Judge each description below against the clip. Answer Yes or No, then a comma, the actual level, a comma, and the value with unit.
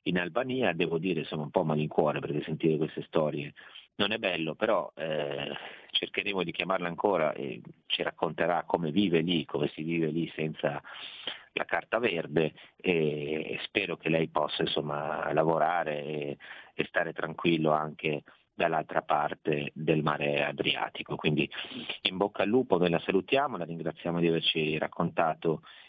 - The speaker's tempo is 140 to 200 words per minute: Yes, average, 150 wpm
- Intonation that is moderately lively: No, narrow, 2.2 semitones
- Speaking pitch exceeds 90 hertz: No, very low, 80 Hz